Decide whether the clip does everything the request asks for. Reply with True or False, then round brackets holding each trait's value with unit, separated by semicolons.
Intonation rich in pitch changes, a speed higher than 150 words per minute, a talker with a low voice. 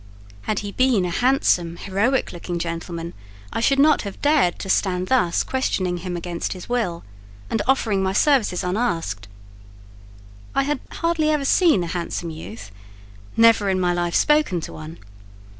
False (7.0 semitones; 160 wpm; 190 Hz)